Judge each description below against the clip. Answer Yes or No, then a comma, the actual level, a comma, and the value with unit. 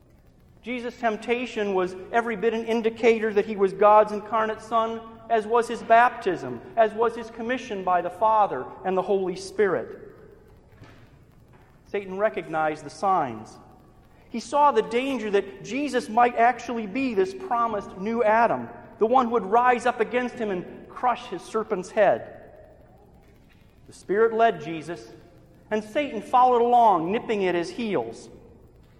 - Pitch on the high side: Yes, high, 225 Hz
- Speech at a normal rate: Yes, average, 145 wpm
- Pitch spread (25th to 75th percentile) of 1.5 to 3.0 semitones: Yes, narrow, 2.6 semitones